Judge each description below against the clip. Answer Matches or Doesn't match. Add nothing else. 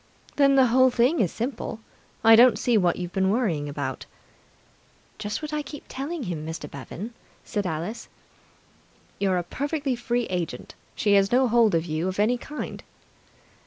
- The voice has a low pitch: Doesn't match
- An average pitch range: Doesn't match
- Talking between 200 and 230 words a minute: Doesn't match